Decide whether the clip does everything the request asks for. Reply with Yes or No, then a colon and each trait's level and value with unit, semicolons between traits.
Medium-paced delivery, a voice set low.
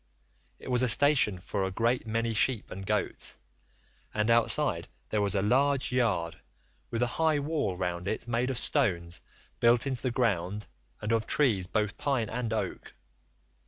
Yes: average, 165 wpm; low, 115 Hz